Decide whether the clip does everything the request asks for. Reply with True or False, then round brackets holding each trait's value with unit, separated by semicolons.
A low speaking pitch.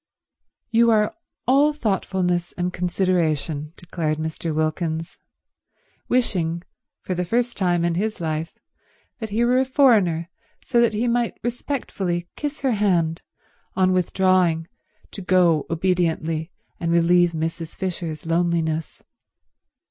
False (180 Hz)